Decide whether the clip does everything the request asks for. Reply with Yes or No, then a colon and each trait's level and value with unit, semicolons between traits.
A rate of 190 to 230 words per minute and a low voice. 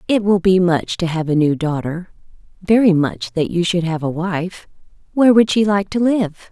No: fast, 205 wpm; medium, 180 Hz